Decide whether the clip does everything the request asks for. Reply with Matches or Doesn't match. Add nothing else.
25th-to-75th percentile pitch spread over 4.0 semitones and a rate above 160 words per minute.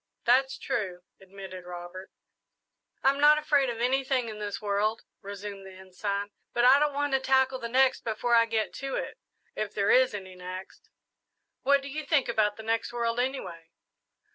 Matches